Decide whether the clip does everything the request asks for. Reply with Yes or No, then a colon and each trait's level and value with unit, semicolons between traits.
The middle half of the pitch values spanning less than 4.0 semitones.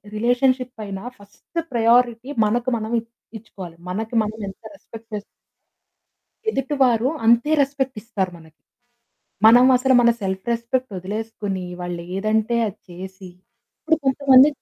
No: average, 4.4 semitones